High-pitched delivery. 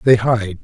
No: low, 110 Hz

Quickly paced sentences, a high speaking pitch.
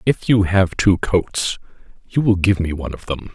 No: fast, 215 wpm; very low, 95 Hz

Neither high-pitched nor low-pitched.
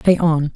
Yes: medium, 160 Hz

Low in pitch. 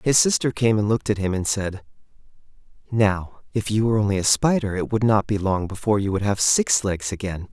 Yes: low, 105 Hz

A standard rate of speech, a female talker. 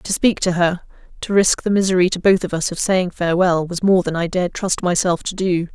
No: fast, 250 wpm; female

